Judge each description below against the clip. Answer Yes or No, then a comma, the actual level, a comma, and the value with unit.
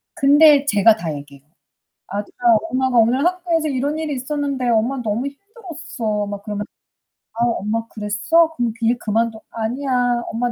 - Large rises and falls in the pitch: No, average, 4.7 semitones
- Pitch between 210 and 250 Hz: Yes, high, 245 Hz